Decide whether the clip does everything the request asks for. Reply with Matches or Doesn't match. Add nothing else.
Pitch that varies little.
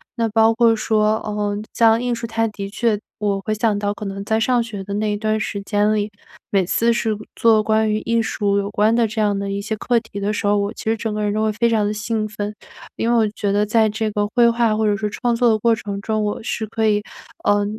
Matches